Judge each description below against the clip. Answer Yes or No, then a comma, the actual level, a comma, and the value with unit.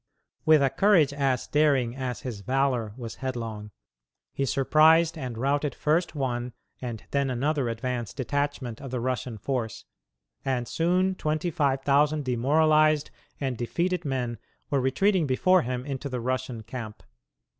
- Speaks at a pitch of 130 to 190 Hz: Yes, low, 135 Hz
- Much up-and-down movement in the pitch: No, average, 3.7 semitones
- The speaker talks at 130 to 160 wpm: Yes, average, 145 wpm